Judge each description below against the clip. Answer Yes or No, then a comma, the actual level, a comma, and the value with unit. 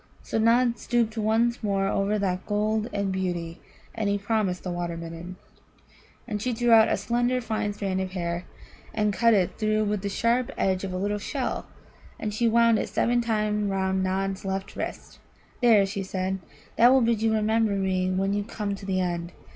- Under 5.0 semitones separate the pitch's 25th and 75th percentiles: Yes, average, 2.9 semitones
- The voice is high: Yes, high, 205 Hz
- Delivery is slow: No, average, 195 wpm